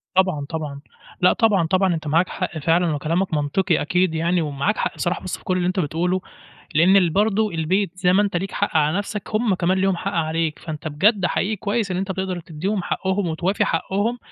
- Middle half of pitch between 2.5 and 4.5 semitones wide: Yes, average, 3.3 semitones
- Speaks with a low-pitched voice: No, medium, 180 Hz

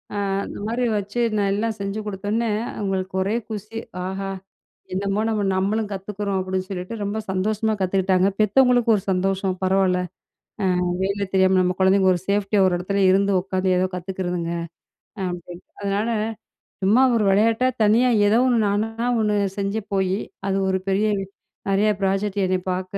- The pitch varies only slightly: Yes, narrow, 2.0 semitones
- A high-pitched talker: Yes, high, 195 Hz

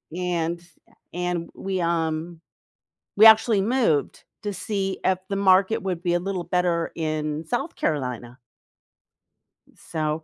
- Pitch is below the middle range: No, medium, 175 Hz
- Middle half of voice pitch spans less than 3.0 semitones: No, average, 3.3 semitones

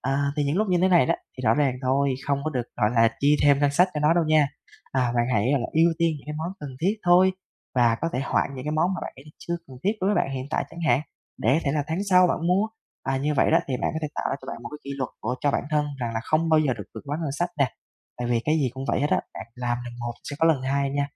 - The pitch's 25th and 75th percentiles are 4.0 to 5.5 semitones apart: No, average, 3.6 semitones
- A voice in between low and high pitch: Yes, medium, 145 Hz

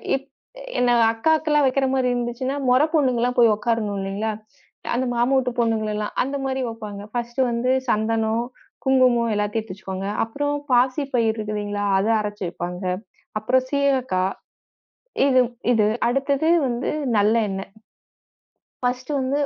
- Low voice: No, high, 235 Hz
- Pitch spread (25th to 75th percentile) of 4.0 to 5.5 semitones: No, average, 3.5 semitones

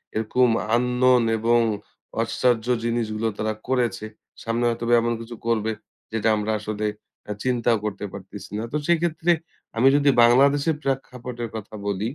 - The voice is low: Yes, low, 120 Hz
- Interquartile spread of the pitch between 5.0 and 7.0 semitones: No, narrow, 2.6 semitones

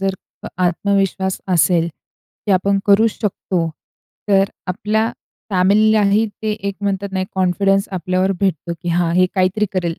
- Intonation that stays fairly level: Yes, narrow, 1.7 semitones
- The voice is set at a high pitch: Yes, high, 195 Hz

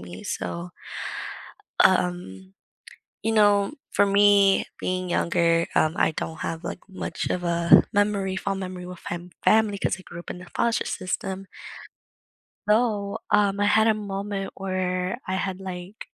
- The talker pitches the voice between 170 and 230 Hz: Yes, high, 190 Hz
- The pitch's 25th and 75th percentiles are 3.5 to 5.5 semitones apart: No, narrow, 2.4 semitones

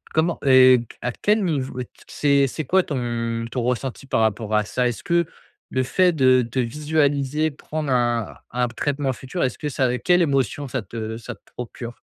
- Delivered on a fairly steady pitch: No, average, 3.6 semitones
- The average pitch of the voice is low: Yes, low, 130 Hz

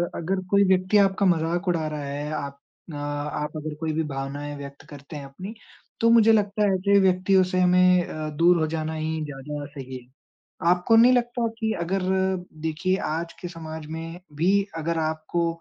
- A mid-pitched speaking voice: Yes, medium, 165 Hz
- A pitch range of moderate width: Yes, average, 3.7 semitones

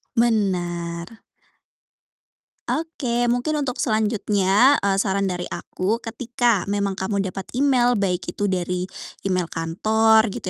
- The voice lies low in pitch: No, high, 205 Hz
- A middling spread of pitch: Yes, average, 4.1 semitones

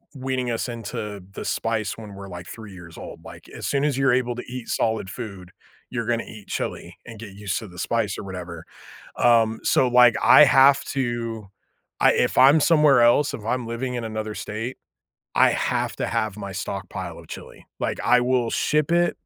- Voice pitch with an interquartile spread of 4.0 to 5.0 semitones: No, average, 3.5 semitones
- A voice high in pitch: No, low, 115 Hz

